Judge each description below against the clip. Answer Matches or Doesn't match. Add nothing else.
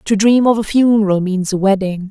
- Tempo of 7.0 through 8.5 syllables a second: Doesn't match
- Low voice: Doesn't match